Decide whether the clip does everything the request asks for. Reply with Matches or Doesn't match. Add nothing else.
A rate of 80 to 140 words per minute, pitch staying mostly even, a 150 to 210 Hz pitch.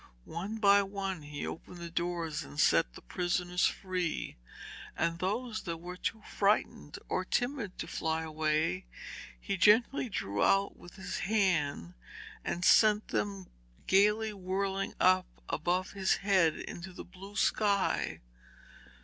Doesn't match